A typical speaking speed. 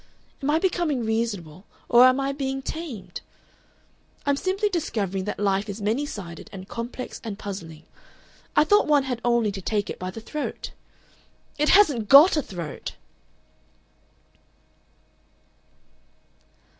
No: slow, 130 wpm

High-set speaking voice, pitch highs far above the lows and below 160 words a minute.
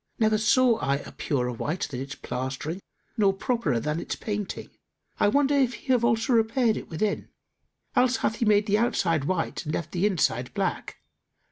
No: high, 205 Hz; wide, 7.2 semitones; average, 180 wpm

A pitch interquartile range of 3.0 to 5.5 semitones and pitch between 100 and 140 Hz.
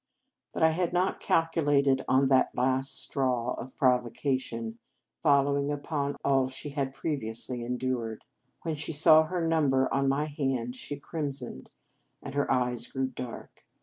No: narrow, 2.5 semitones; low, 135 Hz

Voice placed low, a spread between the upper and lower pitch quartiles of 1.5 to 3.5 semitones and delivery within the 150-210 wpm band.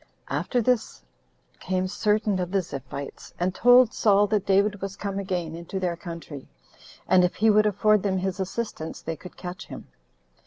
No: high, 190 Hz; average, 2.9 semitones; average, 180 wpm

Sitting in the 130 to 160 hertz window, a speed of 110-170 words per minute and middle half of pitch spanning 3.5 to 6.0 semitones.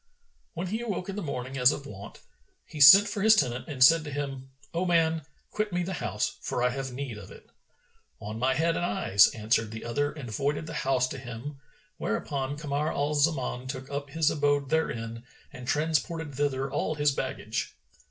No: medium, 140 Hz; average, 195 wpm; average, 4.1 semitones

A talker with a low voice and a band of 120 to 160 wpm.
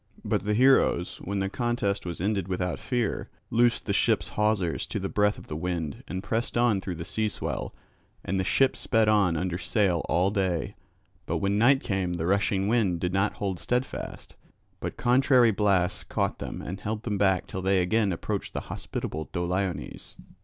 No: low, 100 Hz; average, 185 wpm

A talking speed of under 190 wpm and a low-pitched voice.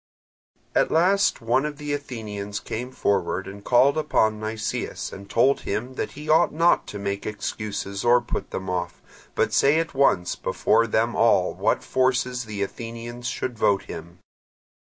Yes: average, 160 wpm; low, 115 Hz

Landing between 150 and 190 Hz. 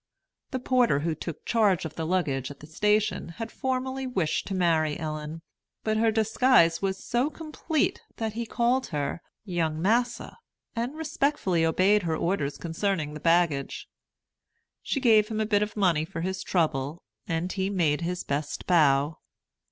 Yes: medium, 185 Hz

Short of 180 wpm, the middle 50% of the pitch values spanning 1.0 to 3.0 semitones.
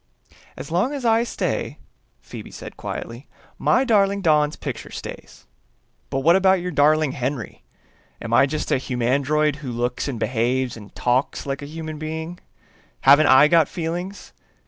No: average, 155 wpm; average, 4.7 semitones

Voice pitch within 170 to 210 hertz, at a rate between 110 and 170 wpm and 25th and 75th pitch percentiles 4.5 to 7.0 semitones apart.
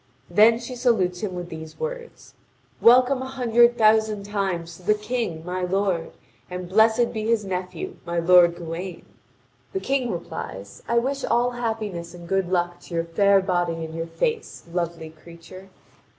Yes: high, 190 Hz; average, 165 wpm; average, 5.2 semitones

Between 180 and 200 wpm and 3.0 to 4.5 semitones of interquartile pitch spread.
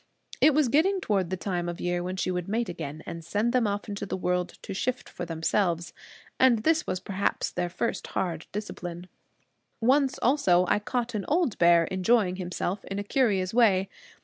No: average, 190 wpm; average, 5.0 semitones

